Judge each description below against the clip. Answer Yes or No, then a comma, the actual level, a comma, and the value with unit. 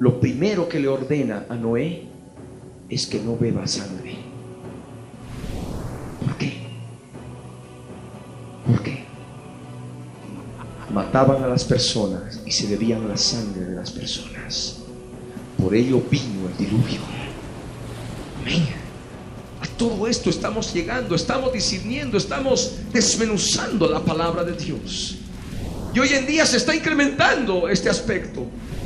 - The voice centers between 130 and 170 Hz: Yes, low, 135 Hz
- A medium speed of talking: No, slow, 115 wpm